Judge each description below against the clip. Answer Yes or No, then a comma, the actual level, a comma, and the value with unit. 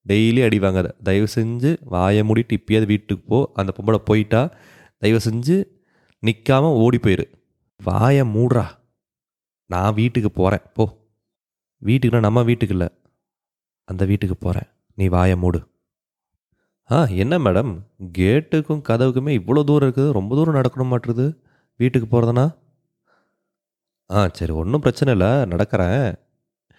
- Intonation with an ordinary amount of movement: Yes, average, 4.6 semitones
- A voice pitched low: Yes, low, 115 Hz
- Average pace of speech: No, slow, 120 wpm